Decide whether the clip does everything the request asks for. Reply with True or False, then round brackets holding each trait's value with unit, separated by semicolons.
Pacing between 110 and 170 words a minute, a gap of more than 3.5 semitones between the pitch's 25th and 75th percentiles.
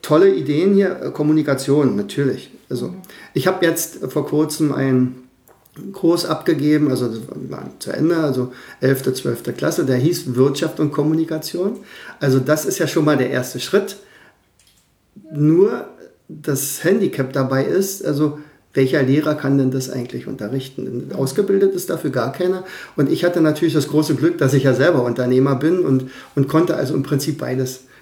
True (160 wpm; 4.0 semitones)